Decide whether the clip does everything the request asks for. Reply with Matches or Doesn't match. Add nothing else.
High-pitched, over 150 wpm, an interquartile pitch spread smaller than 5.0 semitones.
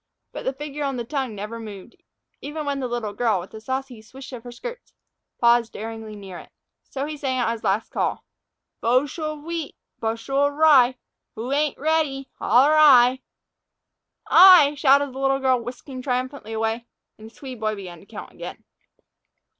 Matches